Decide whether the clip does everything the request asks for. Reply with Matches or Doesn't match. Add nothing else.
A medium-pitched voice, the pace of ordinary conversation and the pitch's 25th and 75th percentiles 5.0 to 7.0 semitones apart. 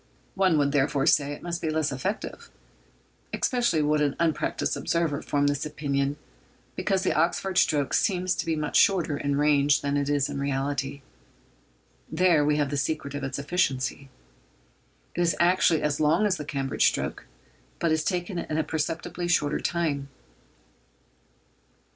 Doesn't match